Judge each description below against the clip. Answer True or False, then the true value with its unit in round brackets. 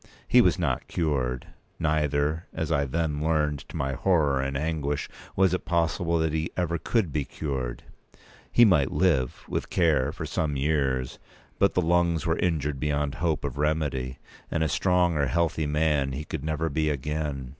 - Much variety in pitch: False (2.7 semitones)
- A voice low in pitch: True (75 Hz)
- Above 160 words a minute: True (175 wpm)